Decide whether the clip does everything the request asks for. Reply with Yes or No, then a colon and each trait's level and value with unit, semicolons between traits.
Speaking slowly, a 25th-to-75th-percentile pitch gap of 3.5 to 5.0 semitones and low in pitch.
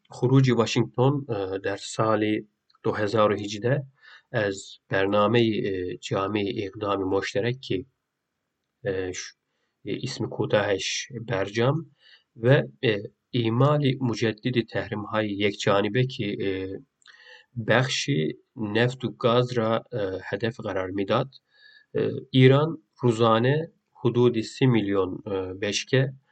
Yes: slow, 90 wpm; average, 4.0 semitones; low, 115 Hz